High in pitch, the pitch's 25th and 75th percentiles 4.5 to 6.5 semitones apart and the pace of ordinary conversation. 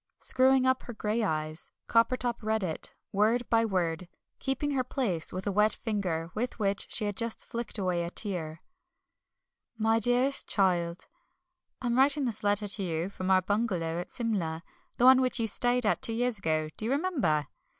Yes: high, 215 Hz; average, 5.2 semitones; average, 180 wpm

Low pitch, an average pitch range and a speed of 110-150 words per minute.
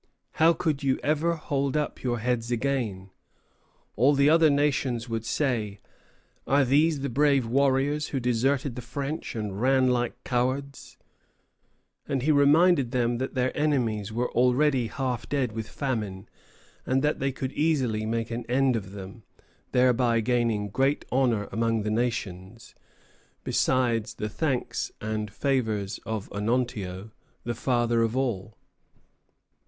Yes: low, 125 Hz; average, 3.6 semitones; average, 140 wpm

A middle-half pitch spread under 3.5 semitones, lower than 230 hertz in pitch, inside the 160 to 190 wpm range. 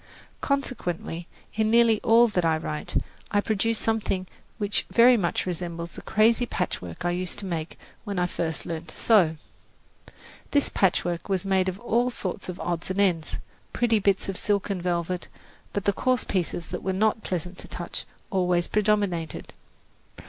No: average, 3.8 semitones; high, 190 Hz; average, 165 wpm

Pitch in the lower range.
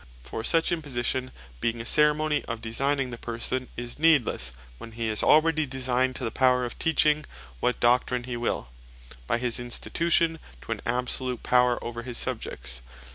Yes: low, 125 Hz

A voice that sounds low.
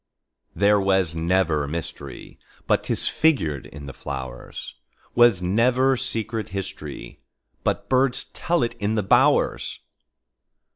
Yes: low, 100 Hz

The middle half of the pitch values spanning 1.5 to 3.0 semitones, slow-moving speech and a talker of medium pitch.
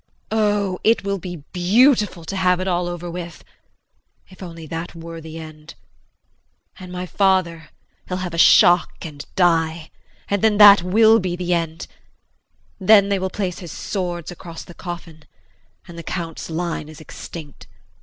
No: narrow, 2.4 semitones; average, 160 wpm; medium, 175 Hz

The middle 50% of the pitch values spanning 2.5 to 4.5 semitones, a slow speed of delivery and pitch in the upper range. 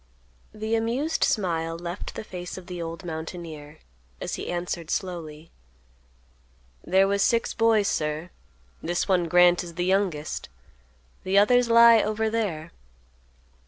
No: average, 4.2 semitones; slow, 130 wpm; medium, 180 Hz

